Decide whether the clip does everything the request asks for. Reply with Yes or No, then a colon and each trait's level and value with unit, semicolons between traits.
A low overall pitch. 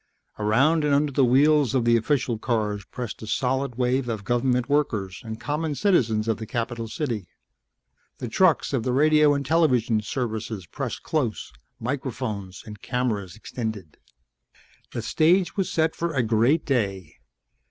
Yes: low, 125 Hz